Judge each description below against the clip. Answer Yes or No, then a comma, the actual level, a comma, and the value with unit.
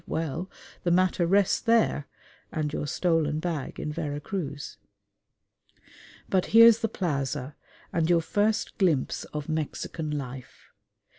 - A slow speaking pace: Yes, slow, 125 wpm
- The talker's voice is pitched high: No, medium, 160 Hz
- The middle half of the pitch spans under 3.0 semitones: No, average, 4.0 semitones